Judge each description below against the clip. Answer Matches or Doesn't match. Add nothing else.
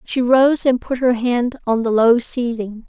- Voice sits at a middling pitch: Doesn't match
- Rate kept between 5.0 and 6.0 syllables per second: Doesn't match